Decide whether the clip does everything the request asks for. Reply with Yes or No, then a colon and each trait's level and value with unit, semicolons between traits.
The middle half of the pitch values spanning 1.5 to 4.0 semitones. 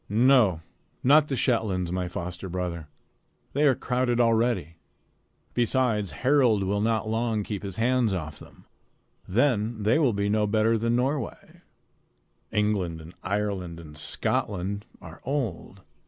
No: average, 4.8 semitones